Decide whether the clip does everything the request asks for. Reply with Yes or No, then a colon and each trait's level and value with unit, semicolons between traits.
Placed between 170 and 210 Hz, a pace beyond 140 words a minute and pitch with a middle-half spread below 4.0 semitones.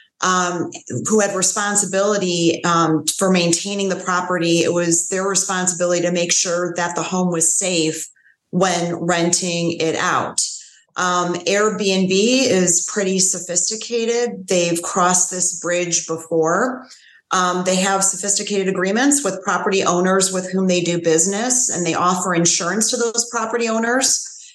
No: medium, 185 Hz; slow, 135 wpm; narrow, 2.5 semitones